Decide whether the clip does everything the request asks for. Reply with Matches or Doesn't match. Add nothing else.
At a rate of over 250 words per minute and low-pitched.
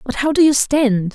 Doesn't match